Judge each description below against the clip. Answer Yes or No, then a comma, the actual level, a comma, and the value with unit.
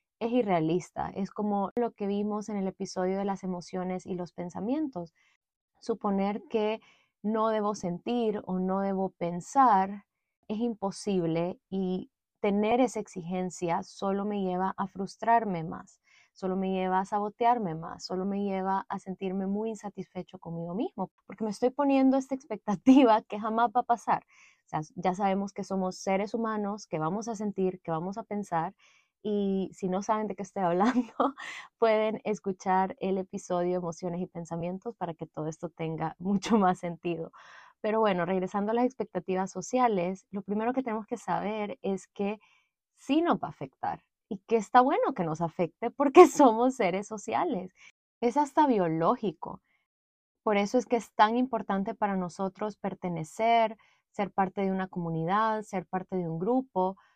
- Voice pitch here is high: Yes, high, 200 Hz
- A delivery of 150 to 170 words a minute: Yes, average, 165 wpm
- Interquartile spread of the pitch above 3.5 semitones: No, average, 3.2 semitones